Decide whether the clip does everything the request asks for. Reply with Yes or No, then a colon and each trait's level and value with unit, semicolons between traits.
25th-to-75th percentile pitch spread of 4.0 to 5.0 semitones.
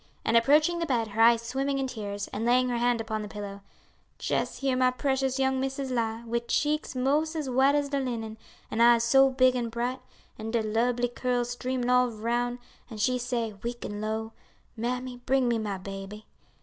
No: average, 2.7 semitones